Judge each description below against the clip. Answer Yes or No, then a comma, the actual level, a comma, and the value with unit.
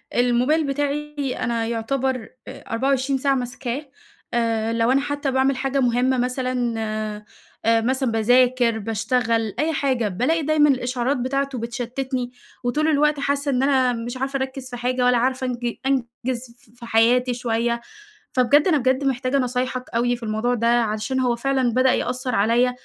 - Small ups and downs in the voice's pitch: Yes, narrow, 2.2 semitones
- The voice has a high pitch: Yes, very high, 250 Hz